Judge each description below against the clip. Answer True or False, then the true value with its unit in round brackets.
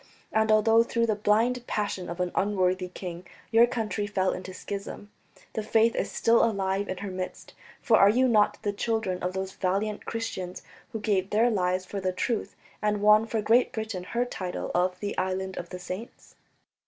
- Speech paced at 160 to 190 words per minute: True (185 wpm)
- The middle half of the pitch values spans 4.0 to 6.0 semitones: False (3.1 semitones)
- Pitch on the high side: True (205 Hz)